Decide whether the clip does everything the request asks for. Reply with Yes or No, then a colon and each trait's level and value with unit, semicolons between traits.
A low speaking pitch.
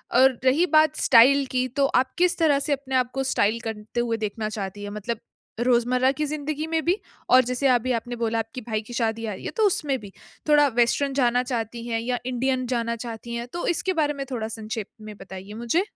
No: high, 245 Hz